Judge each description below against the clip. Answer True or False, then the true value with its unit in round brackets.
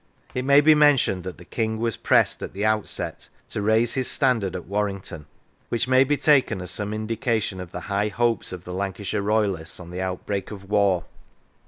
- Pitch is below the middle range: True (105 Hz)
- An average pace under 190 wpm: False (195 wpm)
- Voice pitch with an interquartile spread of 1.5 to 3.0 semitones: False (3.8 semitones)